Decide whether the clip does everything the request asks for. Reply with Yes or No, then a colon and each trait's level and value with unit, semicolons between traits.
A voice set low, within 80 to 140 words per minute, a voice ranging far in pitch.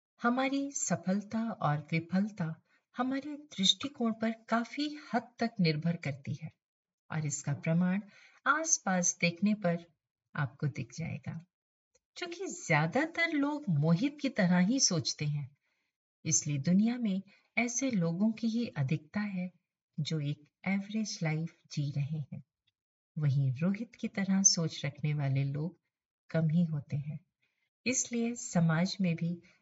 No: medium, 175 Hz; average, 130 wpm; wide, 6.6 semitones